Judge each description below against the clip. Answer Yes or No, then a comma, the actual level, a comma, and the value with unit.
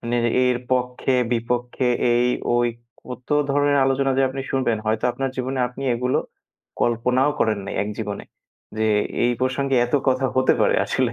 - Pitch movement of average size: No, narrow, 1.7 semitones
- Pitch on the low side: Yes, low, 125 Hz